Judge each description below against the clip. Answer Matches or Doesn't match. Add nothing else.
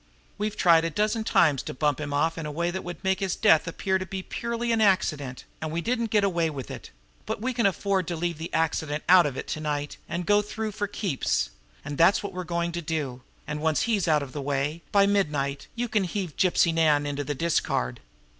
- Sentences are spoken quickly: Matches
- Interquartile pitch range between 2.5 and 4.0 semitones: Doesn't match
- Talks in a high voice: Doesn't match